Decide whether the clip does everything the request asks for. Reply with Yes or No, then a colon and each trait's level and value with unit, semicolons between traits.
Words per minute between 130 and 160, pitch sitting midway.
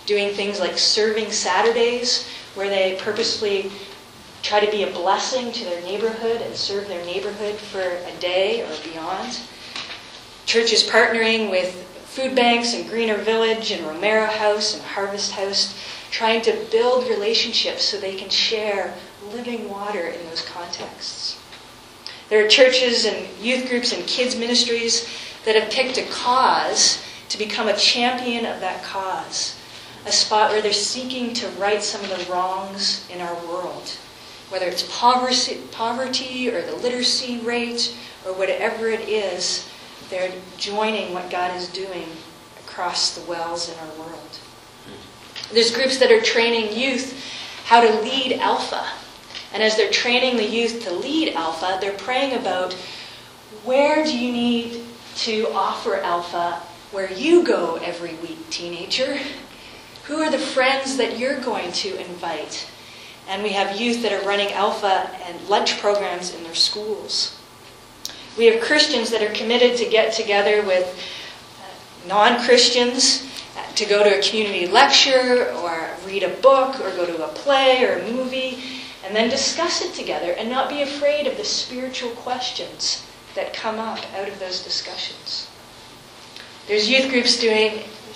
No: average, 150 wpm; high, 220 Hz